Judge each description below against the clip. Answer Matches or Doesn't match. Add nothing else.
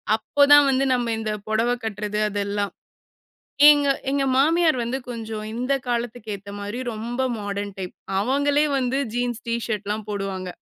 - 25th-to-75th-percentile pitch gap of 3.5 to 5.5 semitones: Matches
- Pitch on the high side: Matches